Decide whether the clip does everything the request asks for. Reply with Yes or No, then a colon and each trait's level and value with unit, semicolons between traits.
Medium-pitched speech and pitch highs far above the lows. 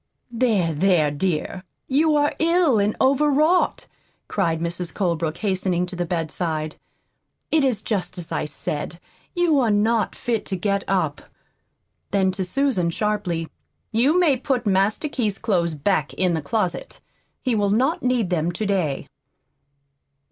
No: high, 195 Hz; wide, 6.3 semitones